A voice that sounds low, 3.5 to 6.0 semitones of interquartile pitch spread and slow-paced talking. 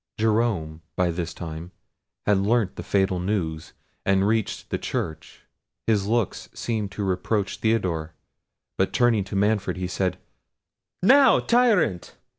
Yes: low, 100 Hz; average, 3.9 semitones; slow, 130 wpm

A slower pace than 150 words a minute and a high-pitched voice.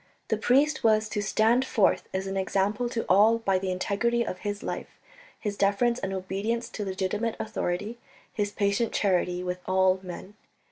No: average, 170 wpm; high, 205 Hz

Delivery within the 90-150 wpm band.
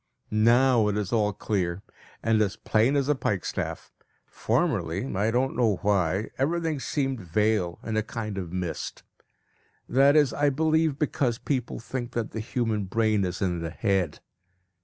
No: average, 160 wpm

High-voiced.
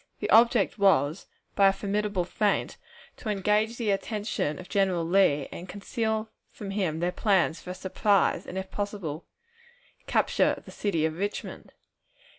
Yes: high, 195 Hz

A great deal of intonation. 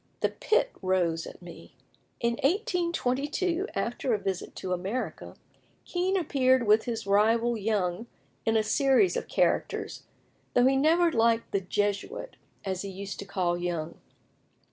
Yes: wide, 6.3 semitones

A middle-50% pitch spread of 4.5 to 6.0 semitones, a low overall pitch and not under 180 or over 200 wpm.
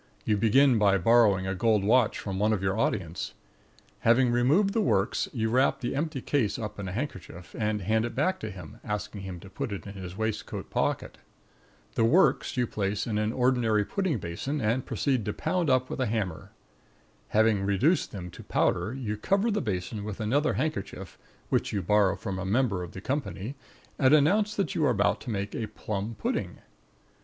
Yes: average, 4.8 semitones; low, 110 Hz; average, 195 wpm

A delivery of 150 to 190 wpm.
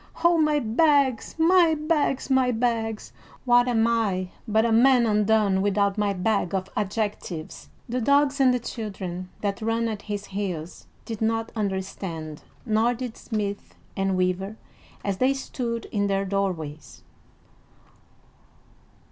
No: slow, 135 wpm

